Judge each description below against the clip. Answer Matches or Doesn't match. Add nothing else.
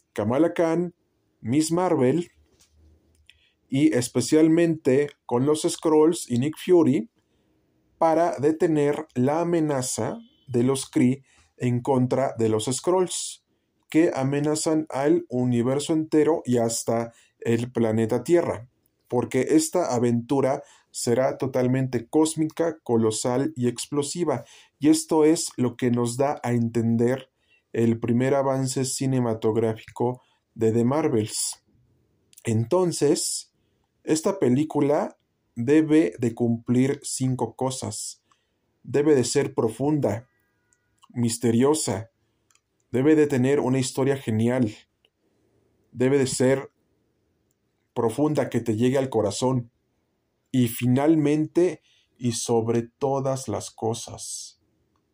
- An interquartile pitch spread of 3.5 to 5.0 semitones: Matches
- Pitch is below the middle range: Matches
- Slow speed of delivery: Matches